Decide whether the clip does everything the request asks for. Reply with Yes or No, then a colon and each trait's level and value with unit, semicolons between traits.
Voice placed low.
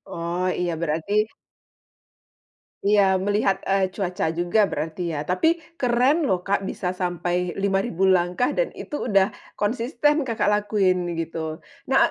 No: high, 190 Hz